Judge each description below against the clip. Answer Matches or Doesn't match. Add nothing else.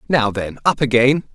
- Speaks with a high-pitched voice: Doesn't match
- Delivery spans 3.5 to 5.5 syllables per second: Matches